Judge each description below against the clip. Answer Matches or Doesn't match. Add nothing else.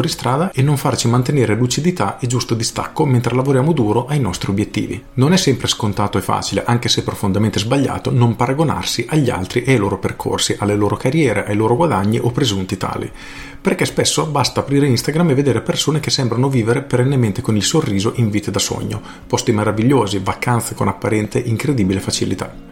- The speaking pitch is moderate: Doesn't match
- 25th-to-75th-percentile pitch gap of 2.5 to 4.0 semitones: Doesn't match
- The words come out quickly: Matches